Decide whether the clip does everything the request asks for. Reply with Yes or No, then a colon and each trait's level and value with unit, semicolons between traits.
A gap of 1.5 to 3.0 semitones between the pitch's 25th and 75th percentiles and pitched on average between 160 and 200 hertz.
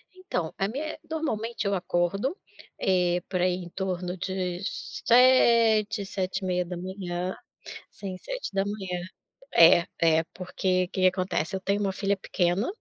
Yes: narrow, 2.5 semitones; high, 190 Hz